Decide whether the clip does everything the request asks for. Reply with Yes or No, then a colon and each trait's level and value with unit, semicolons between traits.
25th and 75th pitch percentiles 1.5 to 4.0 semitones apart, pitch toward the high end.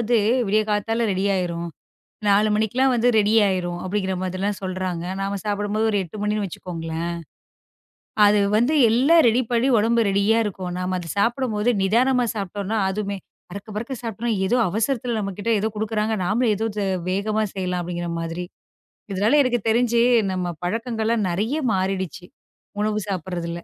Yes: average, 3.3 semitones; high, 205 Hz